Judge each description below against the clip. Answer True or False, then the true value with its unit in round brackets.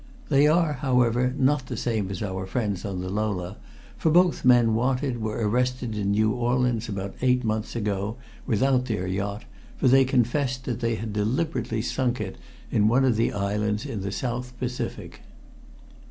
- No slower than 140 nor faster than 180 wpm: True (170 wpm)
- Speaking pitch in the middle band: False (115 Hz)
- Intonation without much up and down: False (3.4 semitones)